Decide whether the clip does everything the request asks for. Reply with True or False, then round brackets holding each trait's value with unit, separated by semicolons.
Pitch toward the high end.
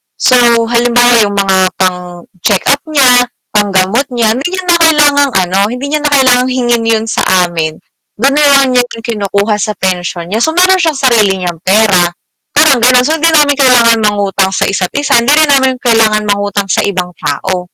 True (230 Hz)